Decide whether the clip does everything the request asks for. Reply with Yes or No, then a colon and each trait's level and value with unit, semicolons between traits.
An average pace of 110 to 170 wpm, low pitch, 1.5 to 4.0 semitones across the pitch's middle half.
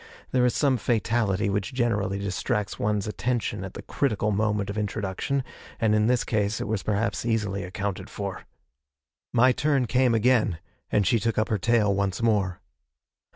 Yes: average, 165 wpm; low, 105 Hz; average, 2.9 semitones